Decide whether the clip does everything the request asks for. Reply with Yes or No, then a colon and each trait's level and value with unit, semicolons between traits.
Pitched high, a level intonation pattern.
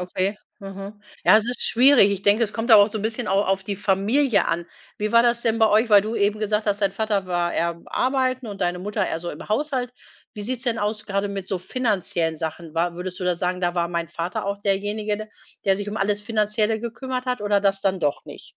No: high, 205 Hz; average, 3.0 semitones